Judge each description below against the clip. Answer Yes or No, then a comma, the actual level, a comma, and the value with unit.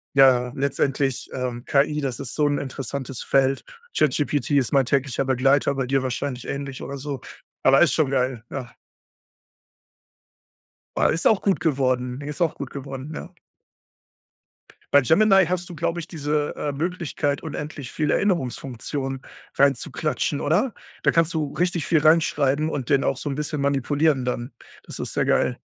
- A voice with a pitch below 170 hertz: Yes, medium, 140 Hz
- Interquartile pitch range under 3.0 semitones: Yes, narrow, 2.6 semitones